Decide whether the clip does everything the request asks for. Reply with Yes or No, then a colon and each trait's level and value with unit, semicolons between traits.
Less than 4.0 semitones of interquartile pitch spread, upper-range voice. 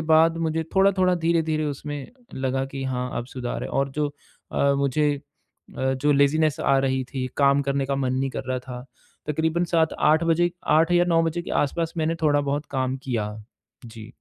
No: average, 3.4 semitones; medium, 145 Hz